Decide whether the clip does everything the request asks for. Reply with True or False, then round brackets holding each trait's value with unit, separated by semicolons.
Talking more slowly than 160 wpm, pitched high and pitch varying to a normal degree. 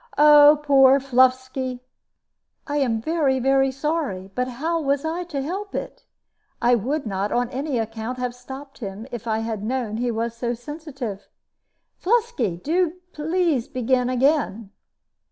True (150 wpm; 260 Hz; 4.1 semitones)